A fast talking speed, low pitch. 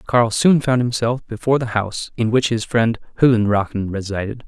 No: average, 175 wpm; low, 115 Hz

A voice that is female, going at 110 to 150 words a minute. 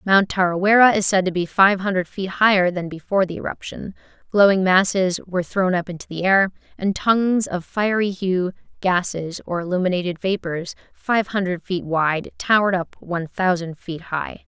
No: female; average, 170 wpm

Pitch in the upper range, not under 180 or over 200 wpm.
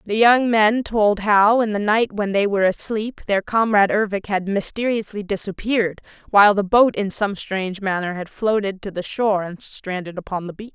Yes: high, 205 Hz; average, 195 wpm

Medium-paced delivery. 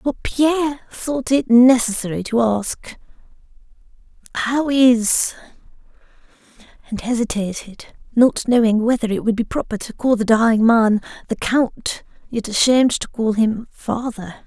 No: slow, 130 wpm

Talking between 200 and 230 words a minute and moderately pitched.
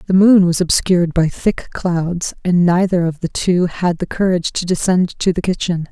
Yes: fast, 205 wpm; medium, 175 Hz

